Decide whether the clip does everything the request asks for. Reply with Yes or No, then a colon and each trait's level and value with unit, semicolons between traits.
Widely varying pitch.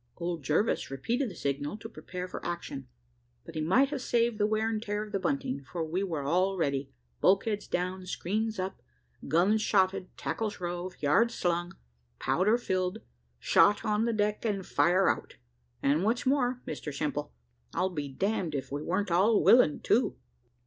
No: average, 4.5 semitones